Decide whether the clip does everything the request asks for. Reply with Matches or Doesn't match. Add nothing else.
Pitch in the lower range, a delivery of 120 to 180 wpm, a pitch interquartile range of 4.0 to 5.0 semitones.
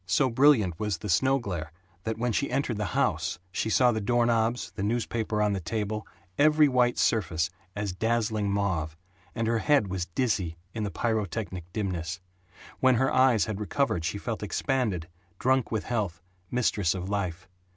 Matches